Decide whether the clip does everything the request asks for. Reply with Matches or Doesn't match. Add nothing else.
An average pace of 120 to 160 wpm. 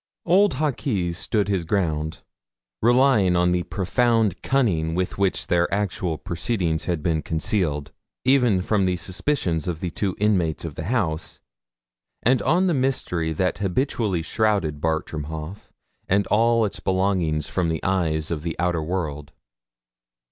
Matches